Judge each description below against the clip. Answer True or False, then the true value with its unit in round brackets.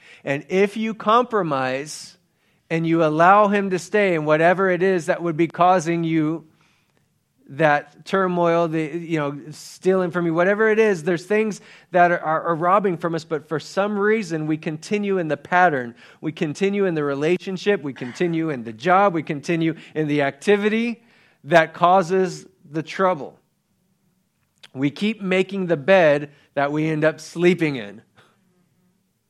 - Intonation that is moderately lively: True (3.5 semitones)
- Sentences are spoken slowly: False (160 wpm)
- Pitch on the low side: False (170 Hz)